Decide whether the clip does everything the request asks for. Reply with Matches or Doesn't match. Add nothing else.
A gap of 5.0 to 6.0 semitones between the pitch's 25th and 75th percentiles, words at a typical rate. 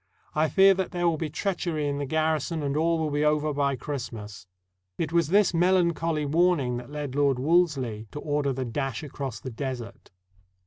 Doesn't match